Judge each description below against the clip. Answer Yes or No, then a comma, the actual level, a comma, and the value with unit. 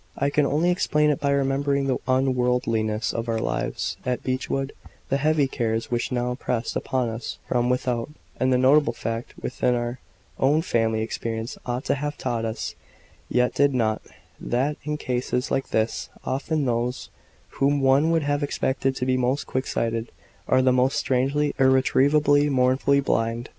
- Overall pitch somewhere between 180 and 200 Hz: No, low, 130 Hz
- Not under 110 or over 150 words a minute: No, average, 165 wpm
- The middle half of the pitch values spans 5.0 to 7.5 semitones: No, narrow, 2.6 semitones